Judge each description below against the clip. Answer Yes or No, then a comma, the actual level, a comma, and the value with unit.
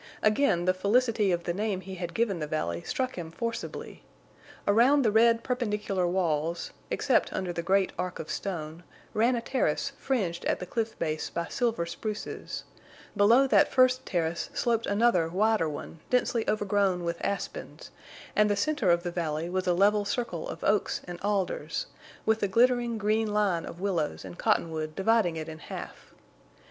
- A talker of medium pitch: No, high, 200 Hz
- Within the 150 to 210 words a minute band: Yes, average, 170 wpm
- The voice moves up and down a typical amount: Yes, average, 4.6 semitones